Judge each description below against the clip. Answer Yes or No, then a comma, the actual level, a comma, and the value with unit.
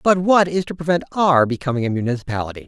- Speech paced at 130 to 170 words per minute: No, average, 200 wpm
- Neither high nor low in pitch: Yes, medium, 145 Hz